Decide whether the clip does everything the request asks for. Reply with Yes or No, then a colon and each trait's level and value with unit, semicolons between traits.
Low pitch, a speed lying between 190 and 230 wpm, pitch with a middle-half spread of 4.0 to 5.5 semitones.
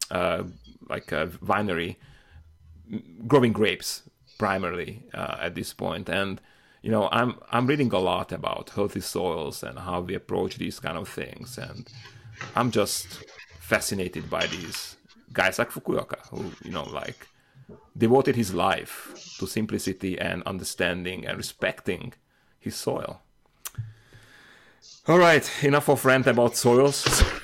No: low, 110 Hz; slow, 135 wpm; average, 4.6 semitones